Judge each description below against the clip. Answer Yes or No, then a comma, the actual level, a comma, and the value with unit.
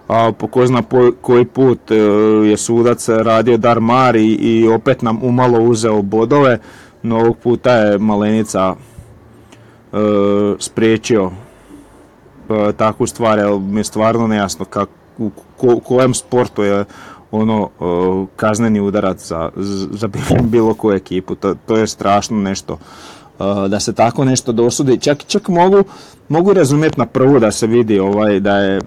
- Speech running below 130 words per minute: No, average, 150 wpm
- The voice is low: Yes, low, 110 Hz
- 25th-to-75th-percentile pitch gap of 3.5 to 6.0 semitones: No, average, 3.0 semitones